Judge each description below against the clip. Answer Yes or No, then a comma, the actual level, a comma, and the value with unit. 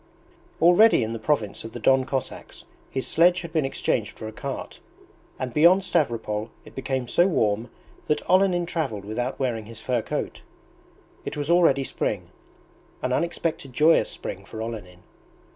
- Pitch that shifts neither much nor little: No, wide, 6.7 semitones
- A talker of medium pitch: No, low, 130 Hz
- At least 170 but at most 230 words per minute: No, average, 160 wpm